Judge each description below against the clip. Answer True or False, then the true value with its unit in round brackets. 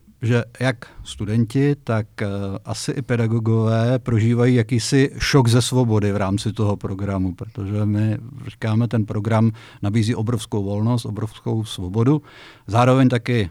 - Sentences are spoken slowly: False (125 wpm)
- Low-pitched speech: True (115 Hz)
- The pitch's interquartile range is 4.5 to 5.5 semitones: False (2.5 semitones)